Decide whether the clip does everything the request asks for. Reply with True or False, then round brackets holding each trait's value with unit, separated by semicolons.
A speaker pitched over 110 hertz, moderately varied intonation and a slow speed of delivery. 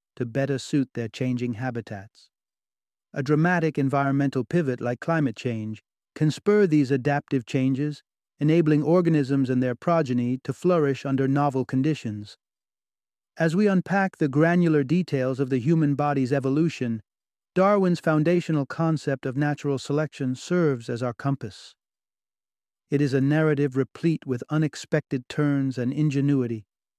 True (140 Hz; 3.3 semitones; 130 wpm)